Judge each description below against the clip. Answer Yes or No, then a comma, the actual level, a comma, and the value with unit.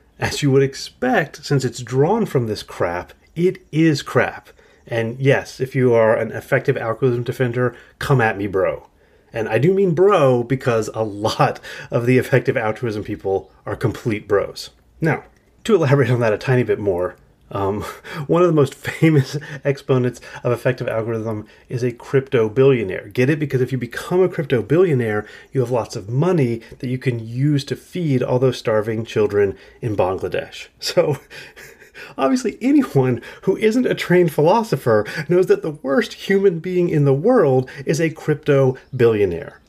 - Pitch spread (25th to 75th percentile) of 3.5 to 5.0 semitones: Yes, average, 4.7 semitones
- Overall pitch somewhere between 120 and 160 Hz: Yes, low, 135 Hz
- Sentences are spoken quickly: No, average, 170 wpm